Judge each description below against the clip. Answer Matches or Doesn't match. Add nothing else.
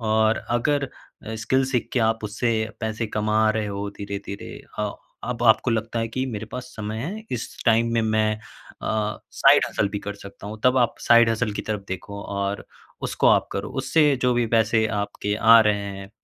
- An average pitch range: Doesn't match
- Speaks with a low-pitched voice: Matches